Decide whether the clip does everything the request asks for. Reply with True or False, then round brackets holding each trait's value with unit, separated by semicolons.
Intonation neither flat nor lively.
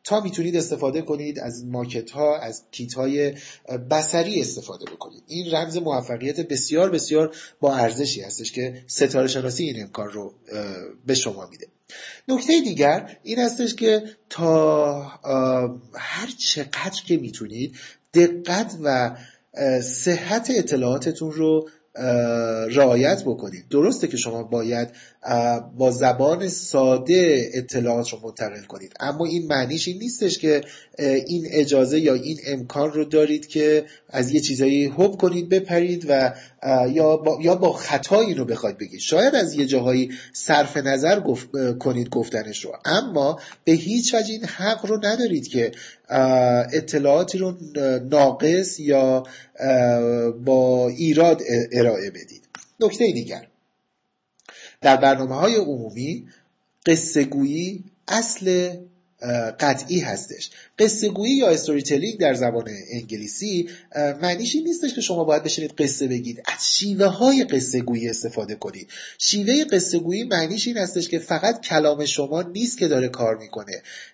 False (5.7 semitones)